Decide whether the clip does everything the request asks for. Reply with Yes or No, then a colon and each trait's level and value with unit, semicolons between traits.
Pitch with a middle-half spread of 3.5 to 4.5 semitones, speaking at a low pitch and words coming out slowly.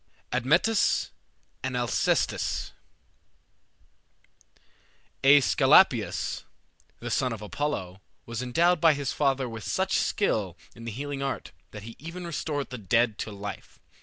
Yes: average, 4.1 semitones; low, 130 Hz; slow, 120 wpm